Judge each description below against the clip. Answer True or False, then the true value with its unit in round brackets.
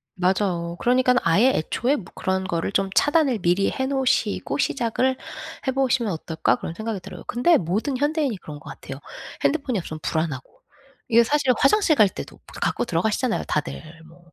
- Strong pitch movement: True (7.2 semitones)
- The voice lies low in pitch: False (220 Hz)